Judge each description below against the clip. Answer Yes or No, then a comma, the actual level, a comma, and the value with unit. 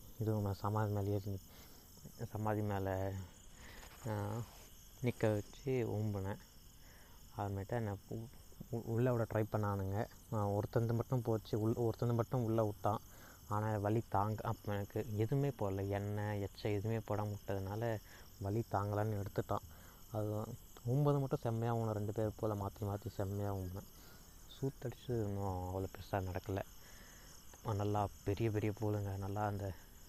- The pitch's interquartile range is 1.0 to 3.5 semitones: Yes, narrow, 2.5 semitones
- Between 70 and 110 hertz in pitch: Yes, low, 105 Hz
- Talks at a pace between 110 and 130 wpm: Yes, average, 125 wpm